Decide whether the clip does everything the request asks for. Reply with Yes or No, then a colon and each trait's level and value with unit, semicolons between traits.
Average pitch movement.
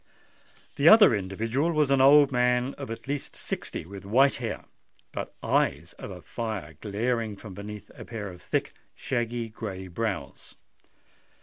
Yes: average, 4.7 semitones